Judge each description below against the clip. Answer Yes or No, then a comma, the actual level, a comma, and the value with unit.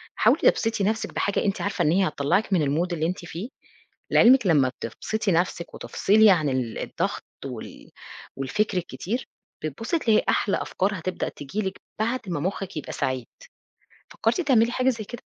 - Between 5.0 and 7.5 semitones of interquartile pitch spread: Yes, wide, 5.4 semitones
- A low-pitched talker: No, high, 190 Hz